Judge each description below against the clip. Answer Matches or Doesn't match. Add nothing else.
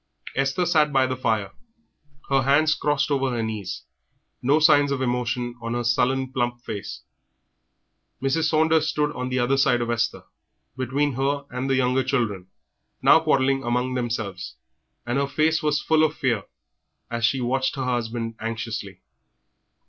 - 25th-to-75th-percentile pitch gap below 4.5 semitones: Matches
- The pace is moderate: Matches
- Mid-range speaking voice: Doesn't match